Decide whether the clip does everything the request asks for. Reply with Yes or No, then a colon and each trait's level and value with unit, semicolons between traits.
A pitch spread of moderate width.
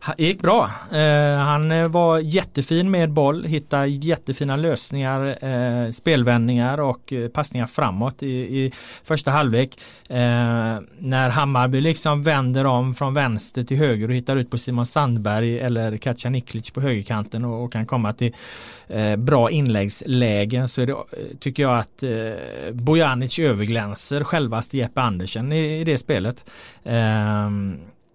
Yes: average, 3.8 semitones